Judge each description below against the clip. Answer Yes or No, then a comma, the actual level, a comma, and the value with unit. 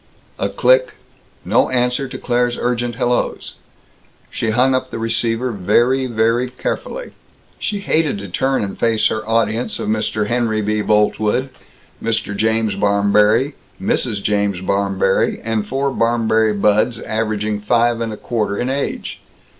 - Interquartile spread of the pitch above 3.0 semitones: No, average, 2.7 semitones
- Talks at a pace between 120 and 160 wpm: Yes, average, 140 wpm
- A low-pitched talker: Yes, low, 115 Hz